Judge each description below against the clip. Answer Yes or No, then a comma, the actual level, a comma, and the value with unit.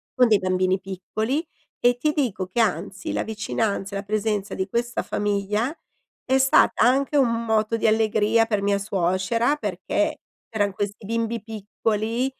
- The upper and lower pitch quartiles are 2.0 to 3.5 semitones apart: Yes, average, 2.8 semitones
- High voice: Yes, high, 215 Hz